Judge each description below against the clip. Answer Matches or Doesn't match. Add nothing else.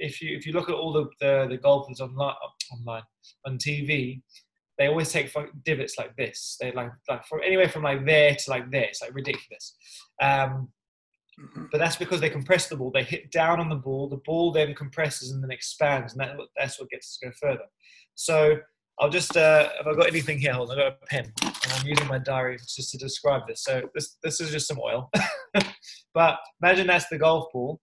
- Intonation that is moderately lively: Matches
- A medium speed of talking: Doesn't match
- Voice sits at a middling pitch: Matches